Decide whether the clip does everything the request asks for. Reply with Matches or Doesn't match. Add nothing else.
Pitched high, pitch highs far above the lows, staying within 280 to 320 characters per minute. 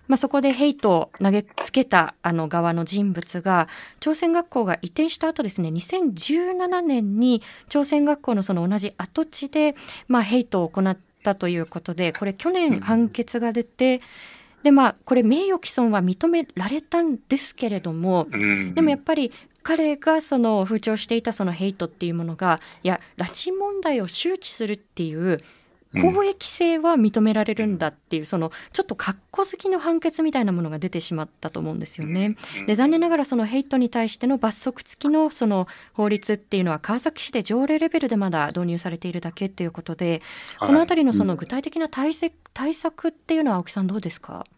Doesn't match